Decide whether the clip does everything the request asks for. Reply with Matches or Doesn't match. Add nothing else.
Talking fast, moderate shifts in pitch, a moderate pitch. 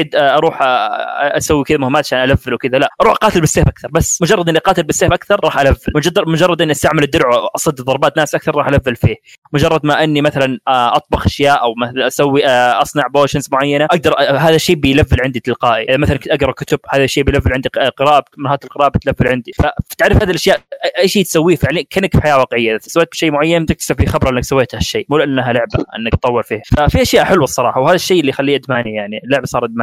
Matches